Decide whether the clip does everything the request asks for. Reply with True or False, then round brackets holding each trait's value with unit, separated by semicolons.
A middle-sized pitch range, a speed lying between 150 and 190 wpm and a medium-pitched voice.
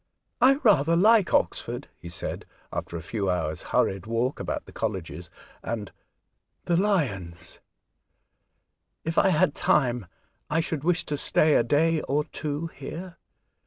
False (8.9 semitones; 155 wpm; 145 Hz)